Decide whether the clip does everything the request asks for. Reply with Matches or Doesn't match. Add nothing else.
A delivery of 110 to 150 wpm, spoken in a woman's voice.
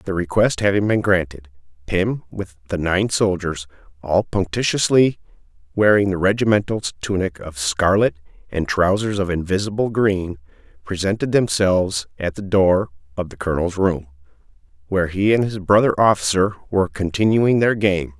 Doesn't match